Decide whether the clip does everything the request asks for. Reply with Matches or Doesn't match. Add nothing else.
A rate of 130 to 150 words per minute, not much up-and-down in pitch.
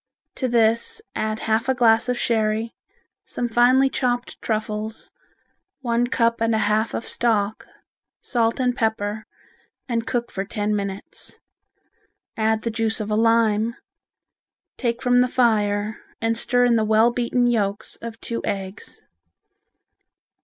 Matches